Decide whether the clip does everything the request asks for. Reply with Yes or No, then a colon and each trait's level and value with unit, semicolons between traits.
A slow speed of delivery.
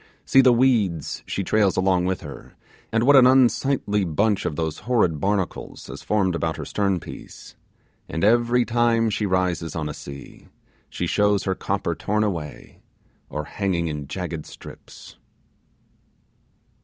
No: average, 150 wpm